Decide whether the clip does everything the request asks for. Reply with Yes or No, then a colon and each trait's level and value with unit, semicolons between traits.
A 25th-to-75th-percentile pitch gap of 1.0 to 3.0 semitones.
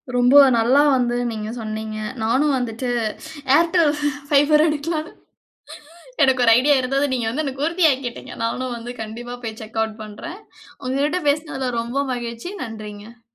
No: average, 4.1 semitones